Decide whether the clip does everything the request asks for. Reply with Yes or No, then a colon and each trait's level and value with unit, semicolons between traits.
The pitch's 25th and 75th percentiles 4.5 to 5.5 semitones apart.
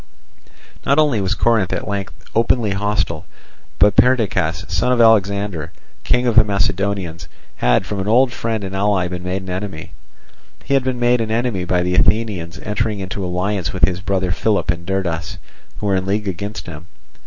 No: average, 3.3 semitones